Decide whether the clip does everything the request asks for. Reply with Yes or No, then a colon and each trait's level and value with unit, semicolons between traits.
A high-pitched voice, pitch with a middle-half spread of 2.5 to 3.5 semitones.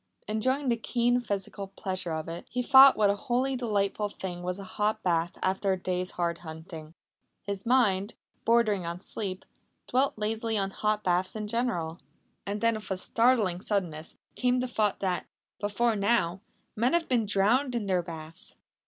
No: high, 205 Hz; average, 4.3 semitones